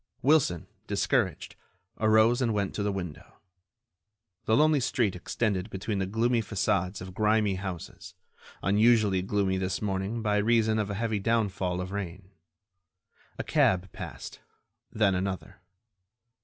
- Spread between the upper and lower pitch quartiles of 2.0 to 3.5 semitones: Yes, average, 2.8 semitones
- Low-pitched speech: Yes, low, 100 Hz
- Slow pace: Yes, slow, 130 wpm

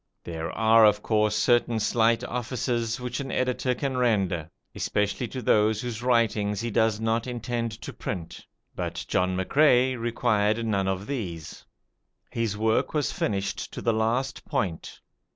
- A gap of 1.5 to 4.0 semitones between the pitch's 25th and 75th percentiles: Yes, average, 2.8 semitones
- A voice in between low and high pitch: No, low, 115 Hz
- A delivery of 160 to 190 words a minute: No, average, 150 wpm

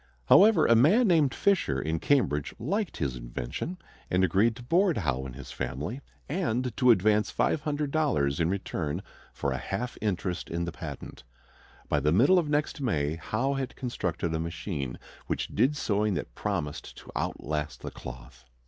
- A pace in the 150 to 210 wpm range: Yes, average, 165 wpm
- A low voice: Yes, low, 100 Hz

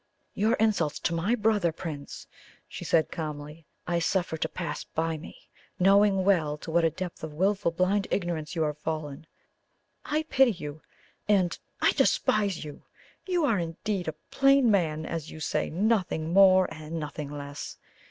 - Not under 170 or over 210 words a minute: No, average, 160 wpm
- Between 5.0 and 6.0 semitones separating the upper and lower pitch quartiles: No, average, 4.3 semitones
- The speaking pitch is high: No, medium, 170 Hz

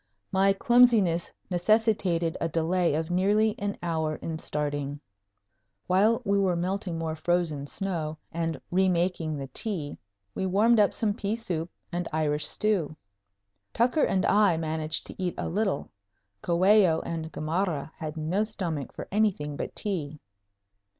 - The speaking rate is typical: Yes, average, 145 wpm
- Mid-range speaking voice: Yes, medium, 175 Hz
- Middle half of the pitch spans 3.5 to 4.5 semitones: Yes, average, 4.0 semitones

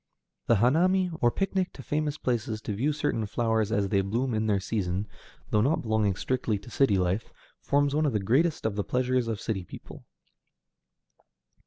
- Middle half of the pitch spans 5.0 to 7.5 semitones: Yes, average, 5.3 semitones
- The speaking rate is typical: Yes, average, 180 wpm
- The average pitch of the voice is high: No, low, 115 Hz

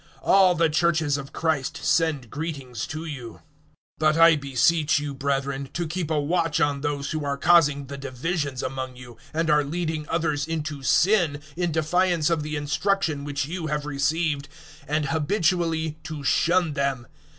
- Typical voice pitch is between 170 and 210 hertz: No, medium, 150 Hz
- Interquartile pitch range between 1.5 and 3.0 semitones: Yes, average, 2.7 semitones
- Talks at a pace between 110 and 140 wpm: No, average, 165 wpm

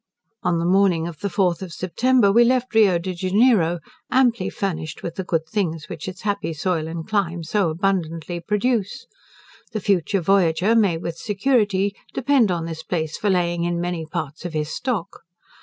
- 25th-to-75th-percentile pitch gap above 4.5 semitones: No, average, 3.7 semitones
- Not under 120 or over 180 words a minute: Yes, average, 175 wpm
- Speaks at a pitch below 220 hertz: Yes, medium, 185 Hz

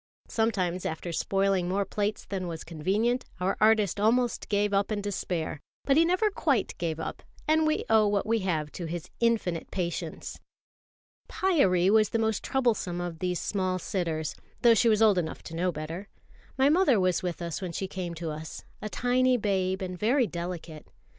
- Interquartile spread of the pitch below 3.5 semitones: No, average, 4.2 semitones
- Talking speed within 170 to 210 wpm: Yes, average, 180 wpm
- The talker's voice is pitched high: Yes, high, 195 Hz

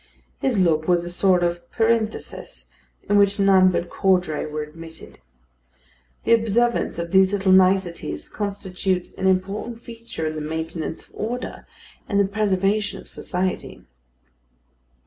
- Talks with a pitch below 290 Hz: Yes, high, 190 Hz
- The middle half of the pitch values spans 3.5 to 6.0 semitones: No, average, 3.0 semitones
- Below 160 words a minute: Yes, slow, 135 wpm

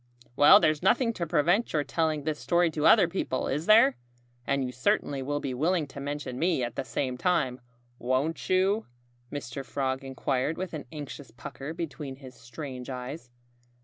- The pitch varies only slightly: No, average, 4.0 semitones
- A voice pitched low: No, medium, 145 Hz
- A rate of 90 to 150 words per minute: No, average, 175 wpm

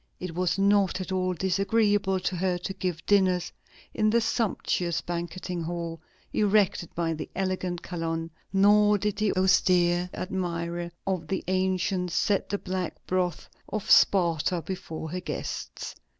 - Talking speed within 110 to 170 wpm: Yes, average, 140 wpm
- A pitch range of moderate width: No, narrow, 2.0 semitones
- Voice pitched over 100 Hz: Yes, medium, 185 Hz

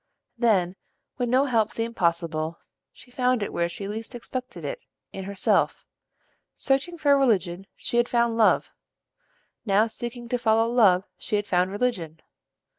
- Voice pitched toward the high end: Yes, high, 225 Hz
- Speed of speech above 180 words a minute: No, average, 145 wpm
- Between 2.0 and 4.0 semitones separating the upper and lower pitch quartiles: No, average, 4.6 semitones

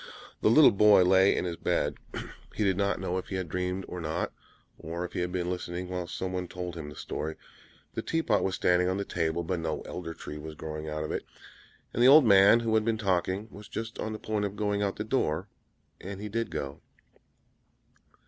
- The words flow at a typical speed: No, fast, 225 wpm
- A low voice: Yes, very low, 95 Hz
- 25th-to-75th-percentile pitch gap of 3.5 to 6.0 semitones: No, average, 3.1 semitones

